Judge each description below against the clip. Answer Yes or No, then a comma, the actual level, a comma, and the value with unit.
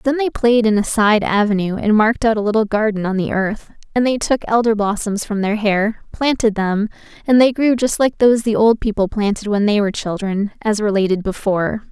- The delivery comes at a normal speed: No, fast, 215 wpm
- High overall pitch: Yes, high, 215 Hz